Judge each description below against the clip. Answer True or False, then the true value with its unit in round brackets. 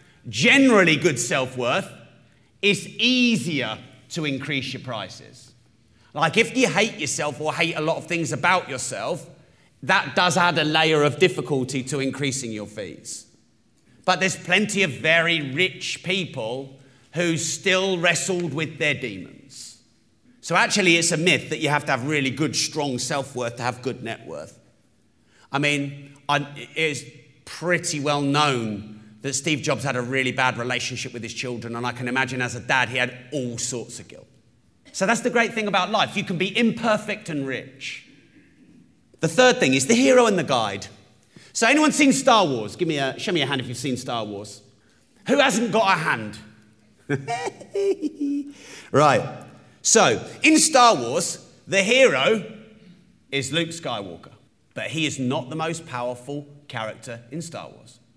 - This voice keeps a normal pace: True (165 wpm)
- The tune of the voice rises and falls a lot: True (6.2 semitones)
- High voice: False (145 Hz)